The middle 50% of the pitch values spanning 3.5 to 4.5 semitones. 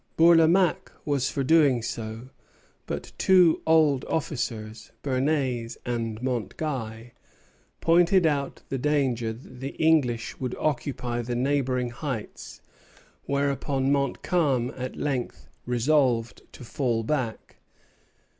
Yes: average, 3.8 semitones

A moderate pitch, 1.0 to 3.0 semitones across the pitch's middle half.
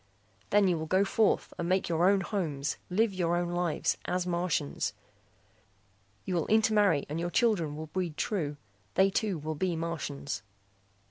No: medium, 175 Hz; average, 3.4 semitones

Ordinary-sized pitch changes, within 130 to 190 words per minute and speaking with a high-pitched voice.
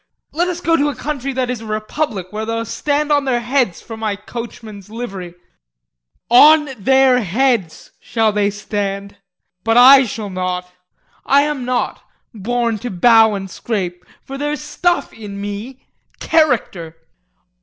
Yes: average, 4.9 semitones; average, 150 wpm; high, 230 Hz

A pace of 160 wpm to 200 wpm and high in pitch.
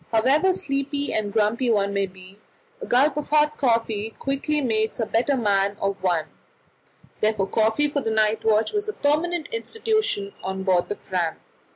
Yes: average, 170 wpm; high, 225 Hz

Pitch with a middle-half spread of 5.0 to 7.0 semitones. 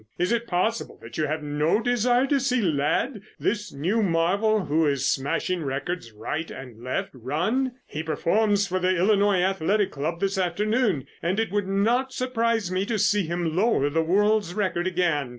Yes: average, 5.3 semitones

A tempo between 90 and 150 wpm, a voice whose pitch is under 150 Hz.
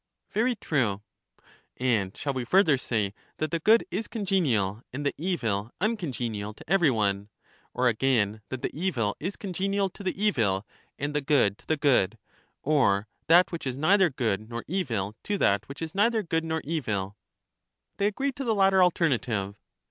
No: average, 170 wpm; medium, 140 Hz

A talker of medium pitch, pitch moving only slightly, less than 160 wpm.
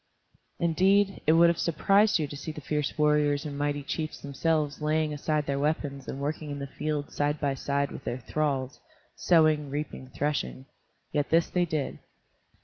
No: medium, 150 Hz; narrow, 1.8 semitones; average, 175 wpm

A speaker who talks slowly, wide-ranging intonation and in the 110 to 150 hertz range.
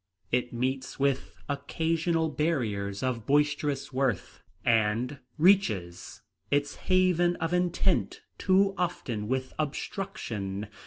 Yes: slow, 100 wpm; wide, 6.0 semitones; medium, 140 Hz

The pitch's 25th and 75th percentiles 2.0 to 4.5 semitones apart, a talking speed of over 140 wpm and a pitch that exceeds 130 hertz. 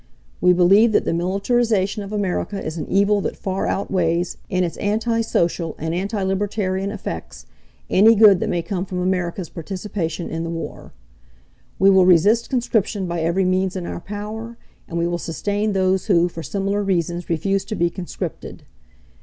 Yes: average, 2.9 semitones; average, 170 wpm; high, 190 Hz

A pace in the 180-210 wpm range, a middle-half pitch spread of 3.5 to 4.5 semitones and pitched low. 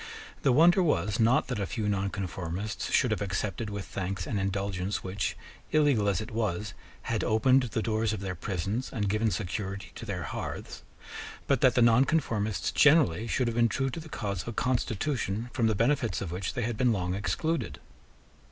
Yes: average, 190 wpm; average, 3.8 semitones; low, 110 Hz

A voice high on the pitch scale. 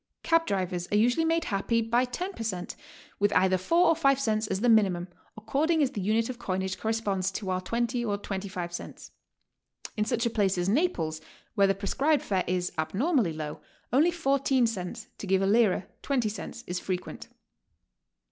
Yes: high, 215 Hz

